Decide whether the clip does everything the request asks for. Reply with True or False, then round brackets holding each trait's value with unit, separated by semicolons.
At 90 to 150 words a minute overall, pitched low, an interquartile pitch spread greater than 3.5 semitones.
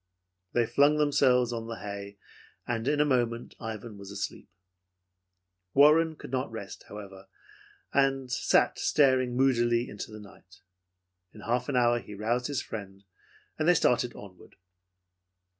True (140 wpm; 120 Hz; 4.2 semitones)